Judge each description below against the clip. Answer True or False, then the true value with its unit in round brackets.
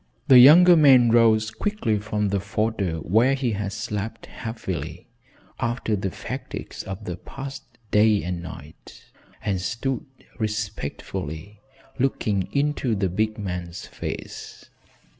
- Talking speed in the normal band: False (120 wpm)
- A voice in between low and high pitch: False (110 Hz)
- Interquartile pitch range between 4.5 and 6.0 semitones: False (3.9 semitones)